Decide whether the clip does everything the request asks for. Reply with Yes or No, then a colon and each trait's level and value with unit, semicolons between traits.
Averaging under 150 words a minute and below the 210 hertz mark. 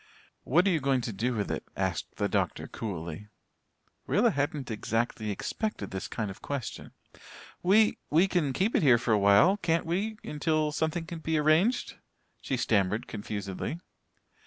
No: average, 160 wpm; medium, 140 Hz